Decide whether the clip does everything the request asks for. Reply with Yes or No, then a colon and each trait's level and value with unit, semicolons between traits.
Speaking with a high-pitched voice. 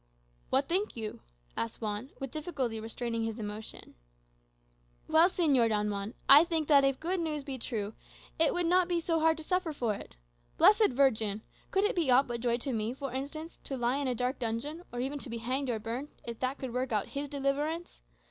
Yes: very high, 265 Hz